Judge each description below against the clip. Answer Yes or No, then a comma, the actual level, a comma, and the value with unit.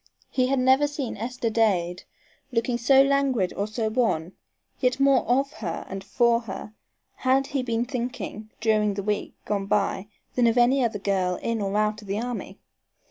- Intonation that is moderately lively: Yes, average, 3.7 semitones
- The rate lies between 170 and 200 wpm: Yes, average, 180 wpm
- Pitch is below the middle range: No, high, 230 Hz